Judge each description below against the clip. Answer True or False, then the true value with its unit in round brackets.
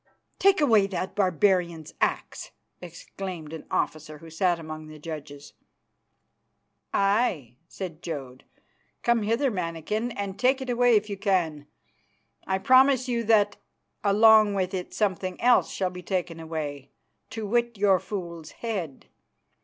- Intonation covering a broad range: False (5.0 semitones)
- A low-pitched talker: False (190 Hz)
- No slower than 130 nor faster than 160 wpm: True (135 wpm)